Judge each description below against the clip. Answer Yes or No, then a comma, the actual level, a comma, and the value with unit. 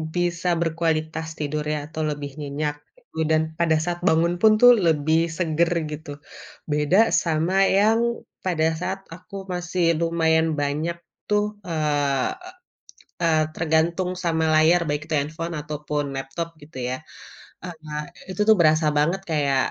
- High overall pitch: No, medium, 160 Hz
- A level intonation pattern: Yes, narrow, 2.3 semitones